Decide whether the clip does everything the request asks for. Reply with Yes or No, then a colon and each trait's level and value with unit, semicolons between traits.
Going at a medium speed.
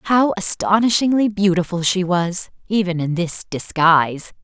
No: slow, 120 wpm